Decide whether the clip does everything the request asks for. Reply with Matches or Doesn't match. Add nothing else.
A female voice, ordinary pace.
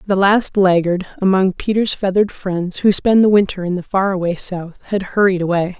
Matches